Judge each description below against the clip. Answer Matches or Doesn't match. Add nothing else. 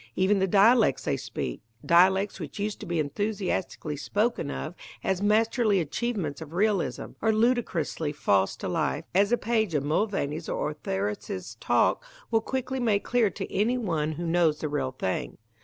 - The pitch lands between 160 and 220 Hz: Matches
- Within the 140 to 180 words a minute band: Matches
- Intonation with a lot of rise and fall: Matches